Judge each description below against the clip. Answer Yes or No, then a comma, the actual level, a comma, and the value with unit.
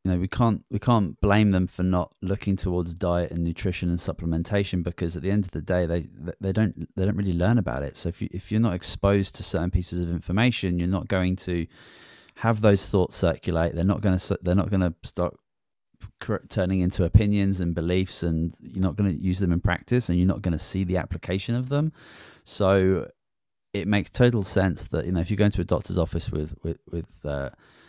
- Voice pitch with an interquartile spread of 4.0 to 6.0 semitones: No, narrow, 2.5 semitones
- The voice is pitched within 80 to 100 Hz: Yes, very low, 95 Hz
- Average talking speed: No, fast, 225 wpm